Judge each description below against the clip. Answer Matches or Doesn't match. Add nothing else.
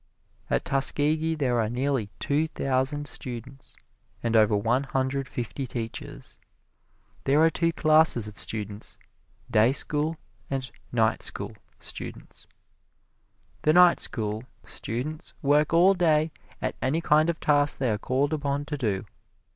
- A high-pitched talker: Doesn't match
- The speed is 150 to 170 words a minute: Doesn't match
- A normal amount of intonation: Matches